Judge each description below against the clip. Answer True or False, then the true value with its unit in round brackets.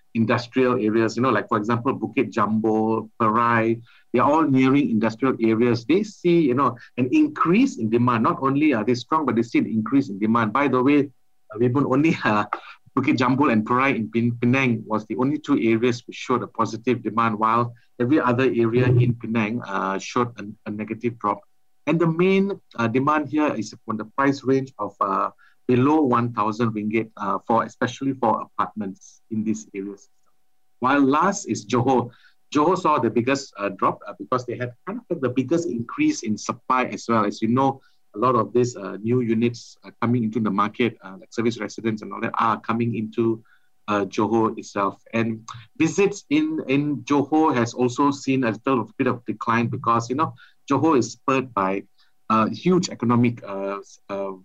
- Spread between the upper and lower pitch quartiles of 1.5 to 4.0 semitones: True (3.3 semitones)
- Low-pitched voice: True (120 Hz)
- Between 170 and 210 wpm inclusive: True (190 wpm)